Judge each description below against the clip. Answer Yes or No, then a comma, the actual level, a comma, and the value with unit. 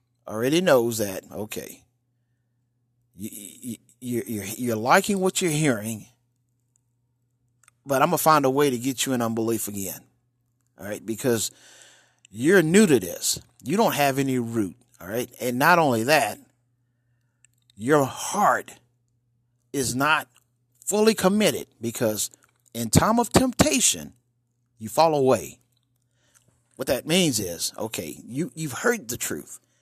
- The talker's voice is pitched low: Yes, low, 120 Hz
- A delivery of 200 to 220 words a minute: No, slow, 135 wpm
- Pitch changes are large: No, narrow, 2.5 semitones